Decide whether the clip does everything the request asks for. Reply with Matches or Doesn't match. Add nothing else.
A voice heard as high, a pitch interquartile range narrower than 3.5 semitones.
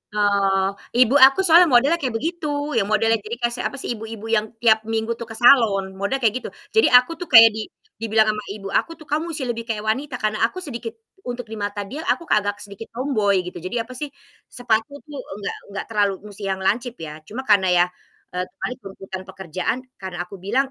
Doesn't match